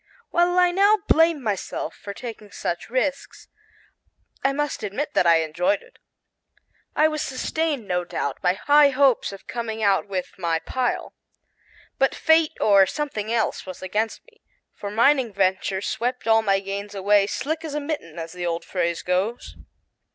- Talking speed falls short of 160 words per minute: No, average, 165 wpm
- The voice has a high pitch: Yes, high, 220 Hz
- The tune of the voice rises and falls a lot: Yes, wide, 7.2 semitones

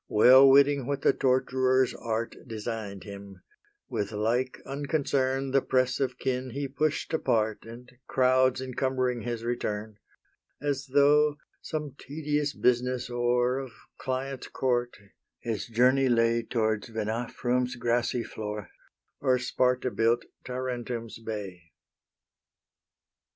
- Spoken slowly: Yes, slow, 115 wpm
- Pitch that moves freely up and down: No, narrow, 2.5 semitones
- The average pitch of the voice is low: Yes, low, 125 Hz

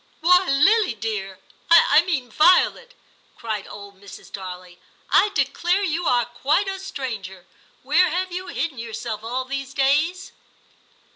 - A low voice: No, very high, 275 Hz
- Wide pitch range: Yes, wide, 8.3 semitones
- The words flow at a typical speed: Yes, average, 155 wpm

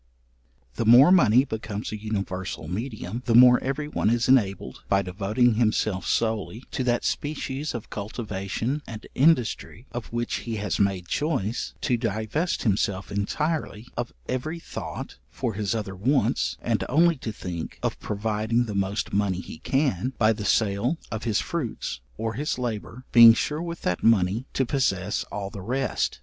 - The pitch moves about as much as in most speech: Yes, average, 4.2 semitones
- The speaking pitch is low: Yes, low, 115 Hz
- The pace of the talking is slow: No, average, 160 wpm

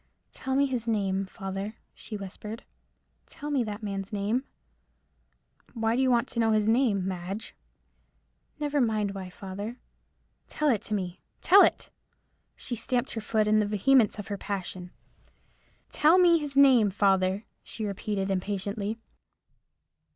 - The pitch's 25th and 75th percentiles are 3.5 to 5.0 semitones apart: Yes, average, 3.8 semitones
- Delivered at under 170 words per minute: Yes, average, 145 wpm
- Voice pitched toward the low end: No, high, 215 Hz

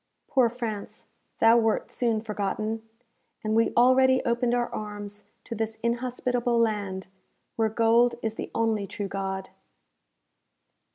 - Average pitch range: No, narrow, 2.2 semitones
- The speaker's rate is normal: No, slow, 125 wpm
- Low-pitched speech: No, high, 225 Hz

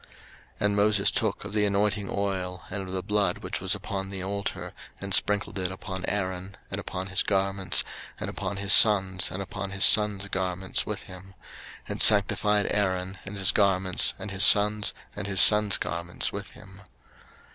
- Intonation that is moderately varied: No, narrow, 1.5 semitones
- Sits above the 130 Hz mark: No, low, 100 Hz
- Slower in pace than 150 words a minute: No, average, 180 wpm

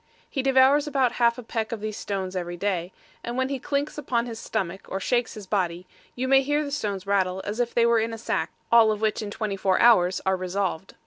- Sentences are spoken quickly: Yes, fast, 240 wpm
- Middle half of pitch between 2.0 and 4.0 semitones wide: No, average, 4.5 semitones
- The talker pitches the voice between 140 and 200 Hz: No, high, 220 Hz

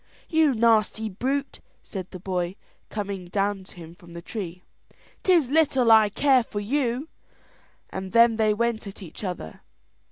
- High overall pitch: Yes, high, 215 Hz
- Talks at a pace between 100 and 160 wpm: Yes, average, 155 wpm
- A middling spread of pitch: Yes, average, 4.3 semitones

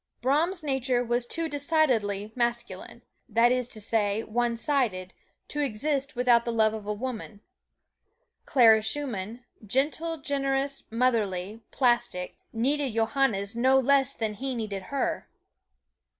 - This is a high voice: Yes, high, 240 Hz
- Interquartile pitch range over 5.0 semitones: No, average, 3.8 semitones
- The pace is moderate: No, slow, 120 wpm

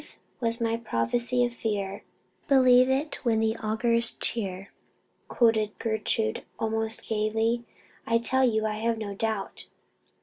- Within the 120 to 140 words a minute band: Yes, slow, 135 wpm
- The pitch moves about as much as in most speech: No, narrow, 1.6 semitones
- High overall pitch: Yes, high, 225 Hz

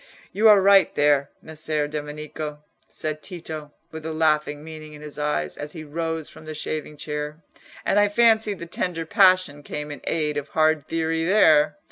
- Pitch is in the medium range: Yes, medium, 155 Hz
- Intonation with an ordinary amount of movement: No, narrow, 1.9 semitones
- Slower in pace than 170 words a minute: No, average, 175 wpm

